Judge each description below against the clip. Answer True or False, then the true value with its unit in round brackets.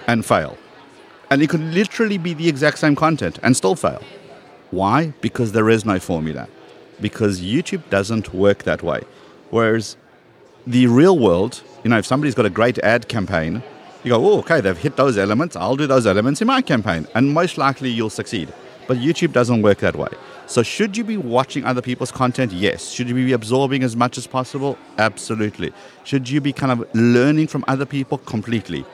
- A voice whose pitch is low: True (125 Hz)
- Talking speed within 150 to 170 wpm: False (195 wpm)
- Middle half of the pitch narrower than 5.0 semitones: True (4.0 semitones)